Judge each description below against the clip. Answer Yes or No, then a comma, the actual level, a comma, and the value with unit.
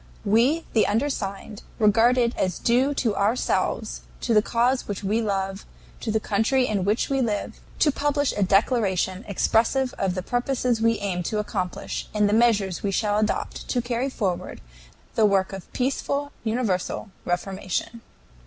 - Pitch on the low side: No, high, 220 Hz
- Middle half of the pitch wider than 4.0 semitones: No, average, 3.7 semitones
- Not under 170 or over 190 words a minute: No, average, 160 wpm